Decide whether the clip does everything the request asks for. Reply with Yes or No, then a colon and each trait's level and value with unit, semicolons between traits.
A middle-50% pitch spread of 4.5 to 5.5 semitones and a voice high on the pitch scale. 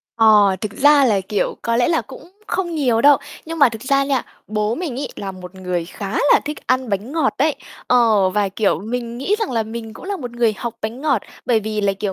Yes: average, 4.8 semitones; high, 230 Hz